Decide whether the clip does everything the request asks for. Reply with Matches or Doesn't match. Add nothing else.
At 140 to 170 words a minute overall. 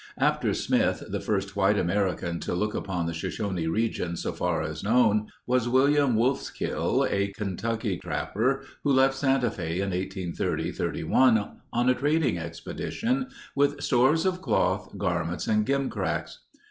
Matches